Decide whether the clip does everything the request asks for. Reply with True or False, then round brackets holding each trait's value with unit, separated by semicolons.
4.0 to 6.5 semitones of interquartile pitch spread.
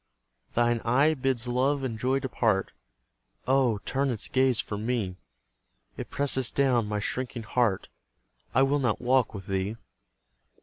False (3.0 semitones)